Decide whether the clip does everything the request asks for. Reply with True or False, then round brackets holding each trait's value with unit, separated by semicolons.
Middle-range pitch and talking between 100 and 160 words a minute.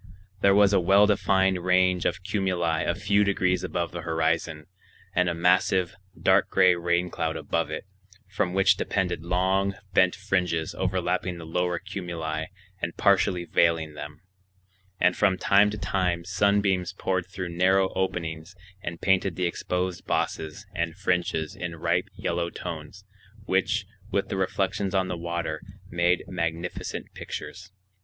False (90 Hz; 145 wpm)